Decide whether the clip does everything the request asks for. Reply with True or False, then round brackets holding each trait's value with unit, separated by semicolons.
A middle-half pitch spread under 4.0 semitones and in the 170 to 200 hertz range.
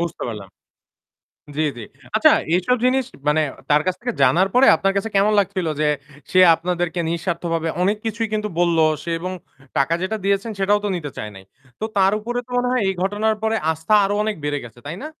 False (4.6 semitones; 185 Hz)